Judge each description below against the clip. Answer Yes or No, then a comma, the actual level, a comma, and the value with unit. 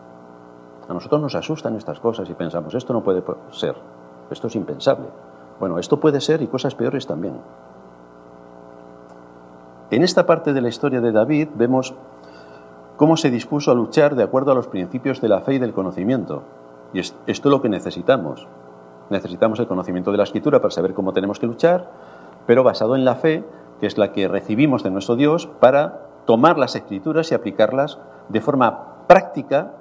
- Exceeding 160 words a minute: Yes, average, 180 wpm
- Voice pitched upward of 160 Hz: No, low, 105 Hz